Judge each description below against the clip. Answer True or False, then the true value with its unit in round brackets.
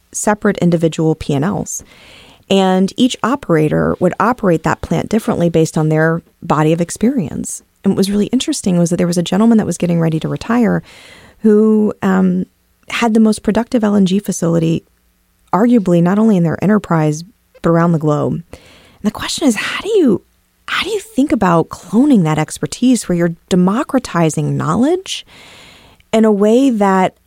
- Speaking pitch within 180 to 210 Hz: True (190 Hz)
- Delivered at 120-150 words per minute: False (165 wpm)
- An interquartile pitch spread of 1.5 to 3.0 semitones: False (5.2 semitones)